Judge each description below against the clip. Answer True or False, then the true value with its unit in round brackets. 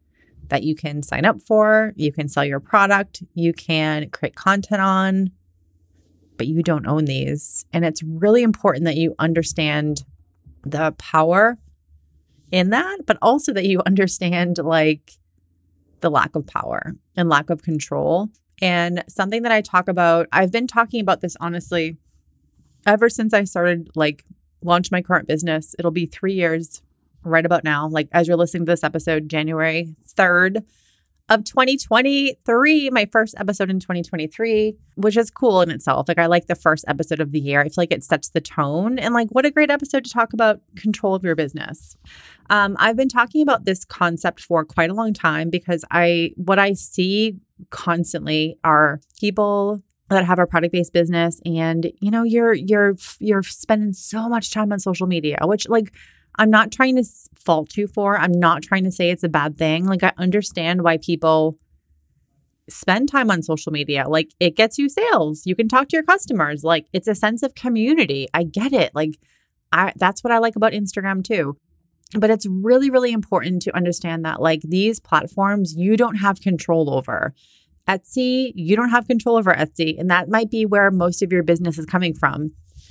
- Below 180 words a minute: False (185 wpm)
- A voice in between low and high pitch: True (175 Hz)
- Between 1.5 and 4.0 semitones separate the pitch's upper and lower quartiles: False (5.0 semitones)